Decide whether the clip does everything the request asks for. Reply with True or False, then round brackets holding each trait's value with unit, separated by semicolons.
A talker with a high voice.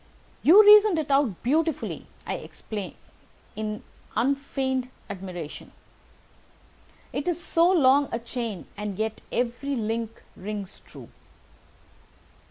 True (250 Hz)